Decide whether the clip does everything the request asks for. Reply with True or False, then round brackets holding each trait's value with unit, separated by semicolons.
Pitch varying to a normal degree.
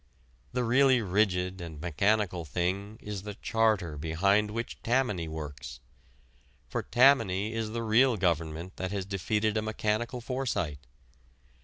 True (4.3 semitones)